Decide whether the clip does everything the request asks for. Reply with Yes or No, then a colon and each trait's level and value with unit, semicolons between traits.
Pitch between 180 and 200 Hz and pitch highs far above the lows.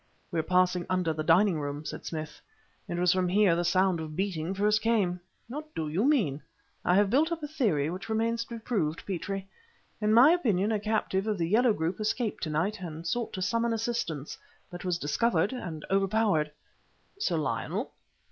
No: high, 190 Hz; average, 4.9 semitones